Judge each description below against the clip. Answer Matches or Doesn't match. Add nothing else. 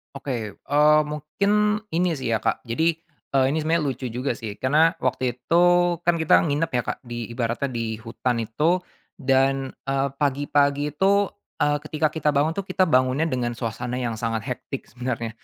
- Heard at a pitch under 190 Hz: Matches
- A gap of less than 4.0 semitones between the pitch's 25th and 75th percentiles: Doesn't match